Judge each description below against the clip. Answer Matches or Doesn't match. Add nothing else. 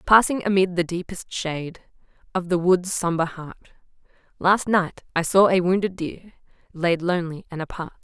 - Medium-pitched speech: Matches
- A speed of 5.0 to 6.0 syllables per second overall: Matches